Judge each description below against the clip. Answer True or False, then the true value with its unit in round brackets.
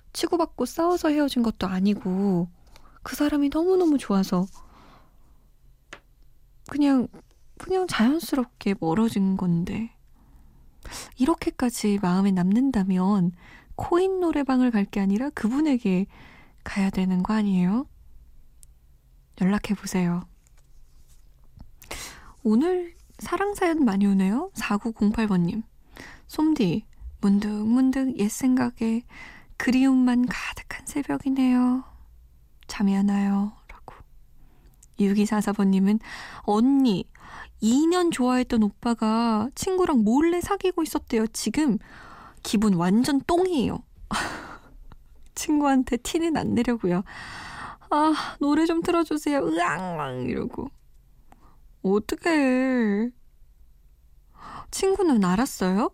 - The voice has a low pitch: False (225 Hz)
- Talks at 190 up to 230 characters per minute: True (210 characters per minute)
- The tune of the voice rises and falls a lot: True (6.8 semitones)